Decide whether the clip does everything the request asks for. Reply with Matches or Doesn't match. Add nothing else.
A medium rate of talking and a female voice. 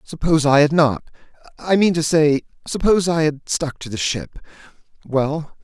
Doesn't match